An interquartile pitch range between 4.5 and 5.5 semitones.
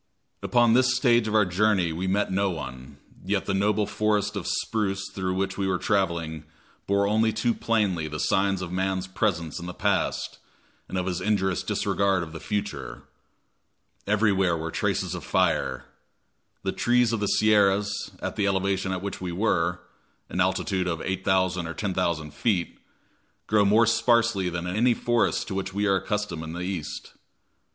No: average, 2.7 semitones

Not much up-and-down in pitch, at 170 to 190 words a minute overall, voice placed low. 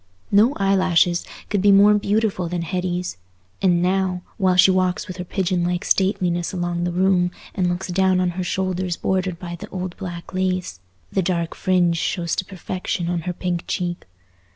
No: narrow, 1.4 semitones; average, 175 wpm; medium, 180 Hz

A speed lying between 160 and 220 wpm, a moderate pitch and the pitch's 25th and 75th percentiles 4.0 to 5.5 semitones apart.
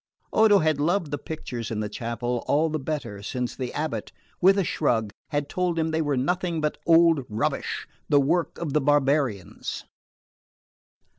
Yes: average, 165 wpm; medium, 145 Hz; average, 4.6 semitones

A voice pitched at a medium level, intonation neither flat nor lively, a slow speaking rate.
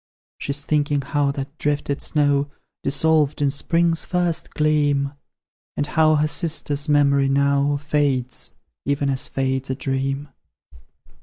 No: medium, 145 Hz; narrow, 1.5 semitones; slow, 125 wpm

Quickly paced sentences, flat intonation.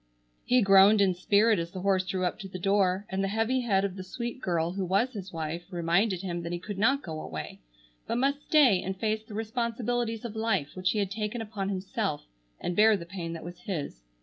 No: fast, 230 wpm; average, 3.5 semitones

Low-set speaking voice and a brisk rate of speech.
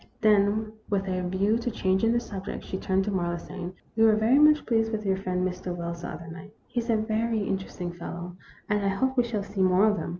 No: high, 200 Hz; fast, 245 wpm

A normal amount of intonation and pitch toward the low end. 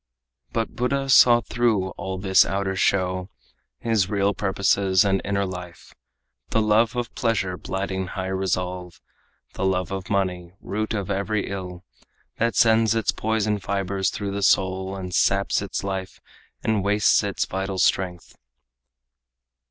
No: narrow, 2.1 semitones; very low, 95 Hz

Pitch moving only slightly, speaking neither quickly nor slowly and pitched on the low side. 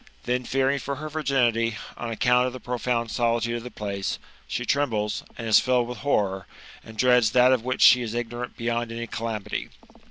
Yes: narrow, 1.7 semitones; average, 190 wpm; low, 120 Hz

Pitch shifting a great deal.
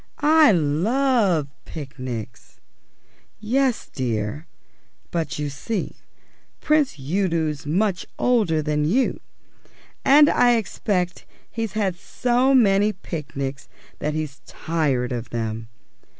Yes: wide, 7.9 semitones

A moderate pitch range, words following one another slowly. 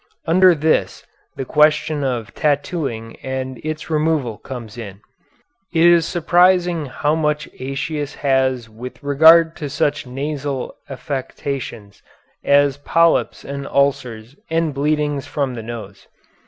Yes: average, 3.3 semitones; slow, 120 wpm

